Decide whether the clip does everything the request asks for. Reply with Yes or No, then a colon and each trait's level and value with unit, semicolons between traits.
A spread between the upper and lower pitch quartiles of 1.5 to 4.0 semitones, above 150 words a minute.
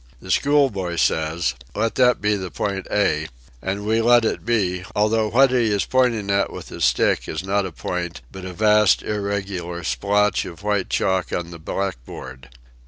Yes: average, 3.3 semitones; average, 190 wpm